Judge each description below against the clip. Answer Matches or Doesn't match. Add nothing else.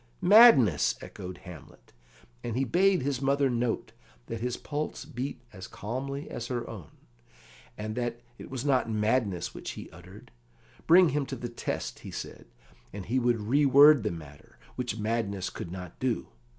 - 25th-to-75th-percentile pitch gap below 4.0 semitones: Doesn't match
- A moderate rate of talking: Matches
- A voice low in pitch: Matches